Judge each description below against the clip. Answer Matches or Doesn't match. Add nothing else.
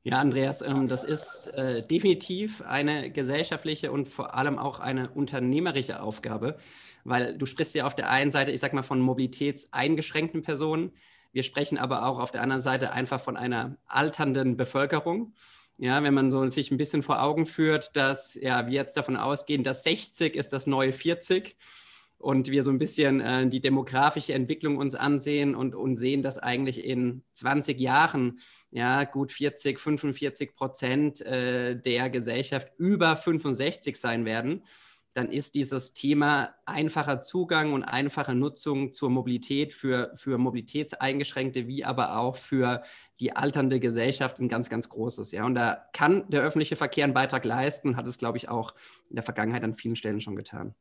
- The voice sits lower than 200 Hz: Matches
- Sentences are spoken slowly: Doesn't match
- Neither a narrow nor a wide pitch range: Doesn't match